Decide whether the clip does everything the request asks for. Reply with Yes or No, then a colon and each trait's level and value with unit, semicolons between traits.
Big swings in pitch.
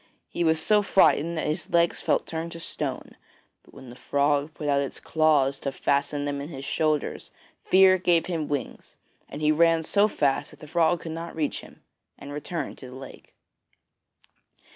No: average, 2.8 semitones